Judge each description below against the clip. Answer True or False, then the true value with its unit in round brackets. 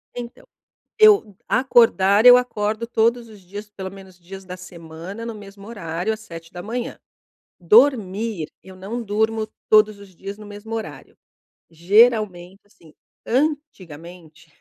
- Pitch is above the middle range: True (205 Hz)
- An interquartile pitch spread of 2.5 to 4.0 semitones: True (3.7 semitones)